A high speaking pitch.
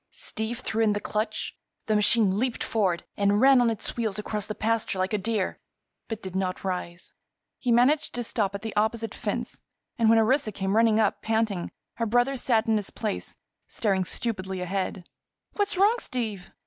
Yes: high, 220 Hz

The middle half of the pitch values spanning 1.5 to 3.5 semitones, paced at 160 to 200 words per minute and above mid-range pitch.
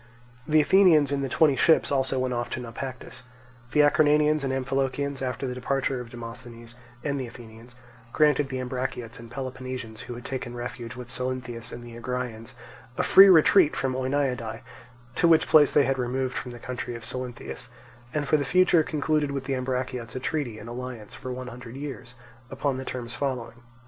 No: narrow, 2.6 semitones; average, 185 wpm; low, 130 Hz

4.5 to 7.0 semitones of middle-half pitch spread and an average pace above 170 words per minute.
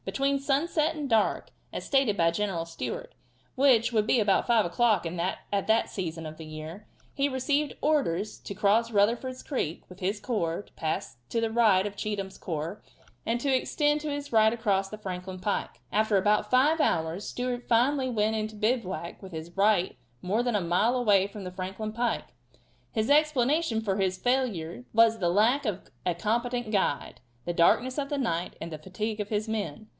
Yes: average, 4.8 semitones; average, 185 wpm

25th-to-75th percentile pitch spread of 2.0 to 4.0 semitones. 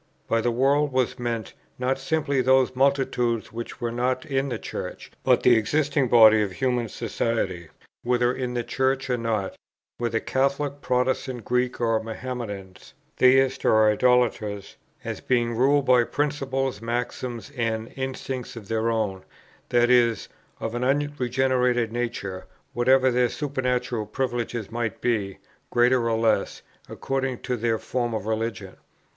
Yes: narrow, 2.4 semitones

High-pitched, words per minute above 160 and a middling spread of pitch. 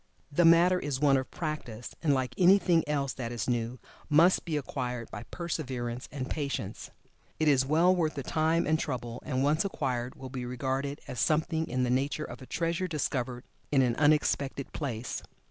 No: medium, 140 Hz; average, 180 wpm; average, 3.8 semitones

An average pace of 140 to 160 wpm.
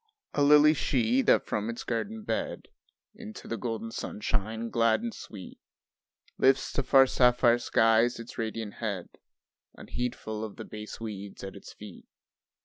Yes: average, 145 wpm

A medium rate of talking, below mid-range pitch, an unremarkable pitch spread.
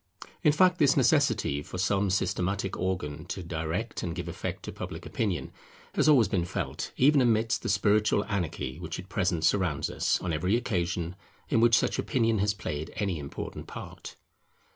Yes: average, 170 wpm; very low, 95 Hz; average, 4.7 semitones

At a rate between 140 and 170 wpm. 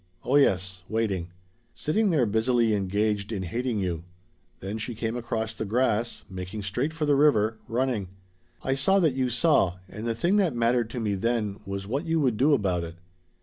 No: average, 190 wpm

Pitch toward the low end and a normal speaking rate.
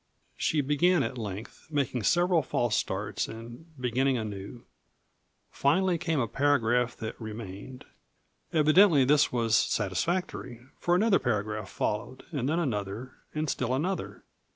No: low, 130 Hz; slow, 130 wpm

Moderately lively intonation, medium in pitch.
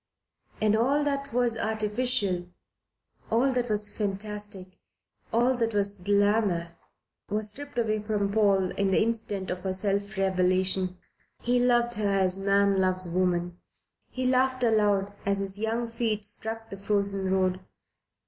No: average, 3.0 semitones; high, 205 Hz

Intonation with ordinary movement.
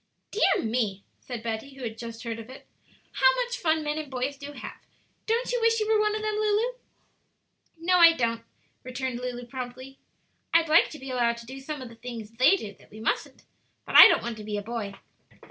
No: wide, 6.2 semitones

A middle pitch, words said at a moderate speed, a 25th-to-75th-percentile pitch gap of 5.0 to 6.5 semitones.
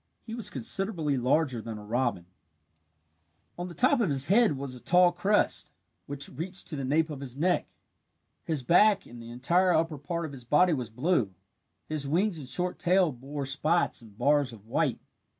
Yes: medium, 150 Hz; average, 185 wpm; wide, 5.5 semitones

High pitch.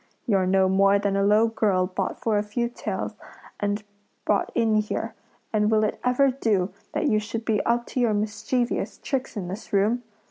Yes: high, 215 Hz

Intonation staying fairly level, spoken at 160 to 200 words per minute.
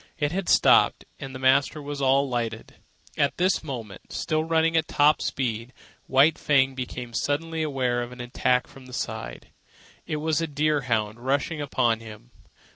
No: average, 3.7 semitones; average, 165 wpm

